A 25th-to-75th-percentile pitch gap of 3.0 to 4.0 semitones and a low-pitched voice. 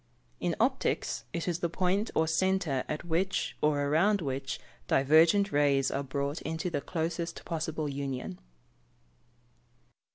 No: average, 3.5 semitones; medium, 160 Hz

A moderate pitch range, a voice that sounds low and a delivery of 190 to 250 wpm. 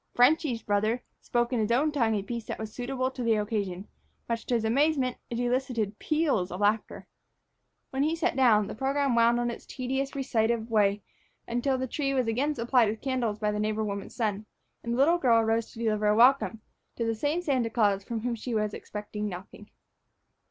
No: average, 3.4 semitones; high, 235 Hz; average, 200 wpm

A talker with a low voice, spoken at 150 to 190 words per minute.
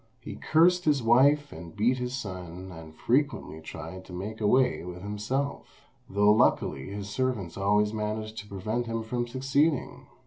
Yes: low, 110 Hz; average, 160 wpm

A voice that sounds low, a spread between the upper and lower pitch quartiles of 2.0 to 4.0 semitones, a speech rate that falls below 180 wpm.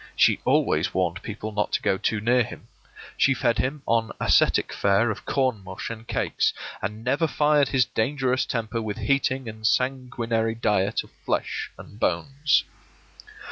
Yes: low, 115 Hz; average, 3.7 semitones; average, 160 wpm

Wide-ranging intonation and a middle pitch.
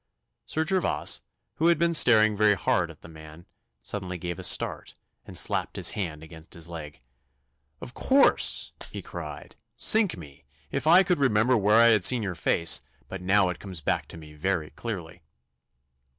No: wide, 6.2 semitones; very low, 95 Hz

